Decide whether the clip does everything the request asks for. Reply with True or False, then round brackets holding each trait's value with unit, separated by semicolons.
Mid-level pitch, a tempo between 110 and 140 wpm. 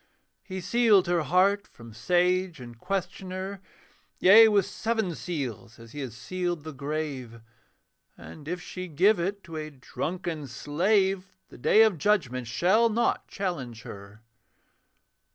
True (175 Hz; 135 wpm)